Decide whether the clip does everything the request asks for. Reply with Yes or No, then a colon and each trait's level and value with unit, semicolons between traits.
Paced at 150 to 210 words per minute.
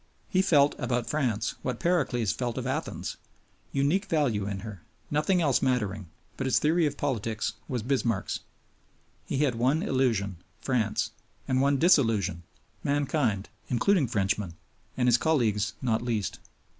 No: average, 140 wpm